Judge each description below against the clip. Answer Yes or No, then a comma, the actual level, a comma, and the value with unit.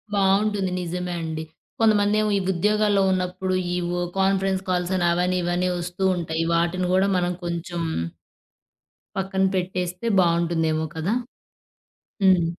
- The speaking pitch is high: No, medium, 180 Hz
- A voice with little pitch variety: Yes, narrow, 2.0 semitones